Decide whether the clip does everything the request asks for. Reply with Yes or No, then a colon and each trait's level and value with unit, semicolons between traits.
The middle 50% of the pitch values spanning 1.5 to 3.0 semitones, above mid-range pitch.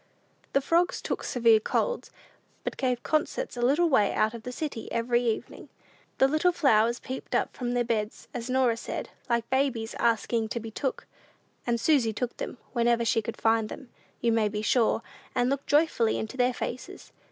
Yes: average, 2.7 semitones; high, 240 Hz